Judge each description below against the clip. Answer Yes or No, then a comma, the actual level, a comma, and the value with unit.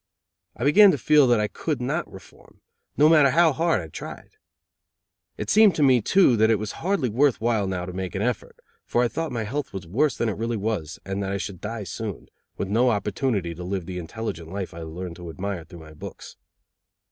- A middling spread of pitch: No, wide, 6.2 semitones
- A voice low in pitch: Yes, low, 110 Hz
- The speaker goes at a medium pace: No, fast, 225 wpm